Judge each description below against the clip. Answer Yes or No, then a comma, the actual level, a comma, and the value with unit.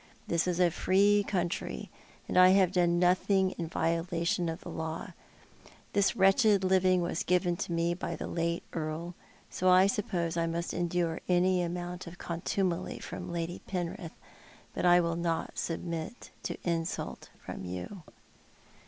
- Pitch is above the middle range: No, medium, 175 Hz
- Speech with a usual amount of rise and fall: No, narrow, 1.7 semitones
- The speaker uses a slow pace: No, average, 155 wpm